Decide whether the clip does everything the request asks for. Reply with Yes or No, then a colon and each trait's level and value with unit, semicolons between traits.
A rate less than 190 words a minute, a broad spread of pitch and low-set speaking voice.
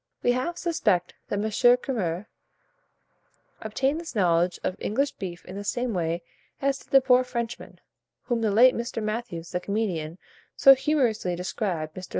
No: average, 155 wpm; wide, 5.9 semitones; high, 220 Hz